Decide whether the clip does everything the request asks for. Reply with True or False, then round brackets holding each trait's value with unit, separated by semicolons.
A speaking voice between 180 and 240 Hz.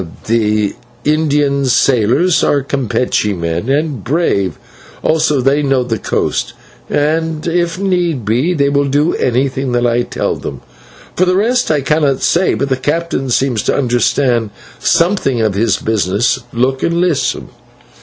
False (140 Hz)